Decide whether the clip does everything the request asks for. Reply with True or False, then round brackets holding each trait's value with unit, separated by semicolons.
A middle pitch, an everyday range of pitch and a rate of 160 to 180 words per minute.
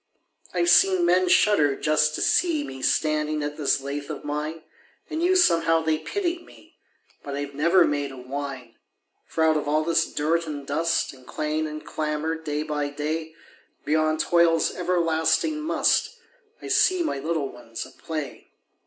False (155 Hz; 2.3 semitones; 170 wpm)